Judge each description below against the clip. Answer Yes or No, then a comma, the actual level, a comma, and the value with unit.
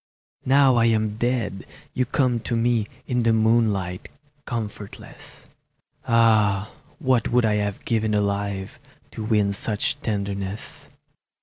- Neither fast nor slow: No, slow, 120 wpm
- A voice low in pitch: Yes, low, 110 Hz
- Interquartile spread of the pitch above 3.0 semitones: No, narrow, 2.6 semitones